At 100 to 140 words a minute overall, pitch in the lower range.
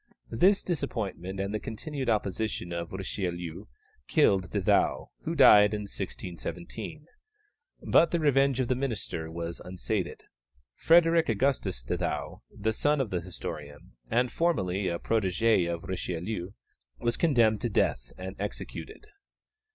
Yes: slow, 135 wpm; low, 105 Hz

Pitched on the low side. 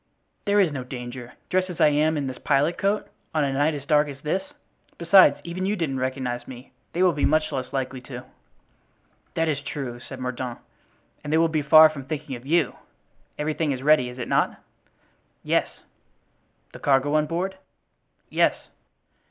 No: medium, 145 Hz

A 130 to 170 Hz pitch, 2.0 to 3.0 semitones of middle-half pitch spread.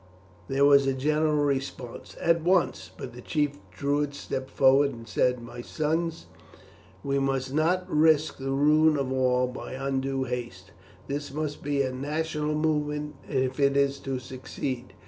Yes: medium, 140 Hz; narrow, 2.4 semitones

